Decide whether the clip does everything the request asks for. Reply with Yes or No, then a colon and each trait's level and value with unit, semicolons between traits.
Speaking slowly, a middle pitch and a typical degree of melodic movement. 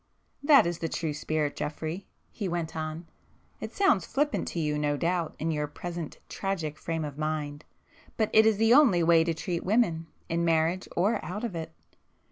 No: average, 170 wpm; medium, 165 Hz; average, 3.9 semitones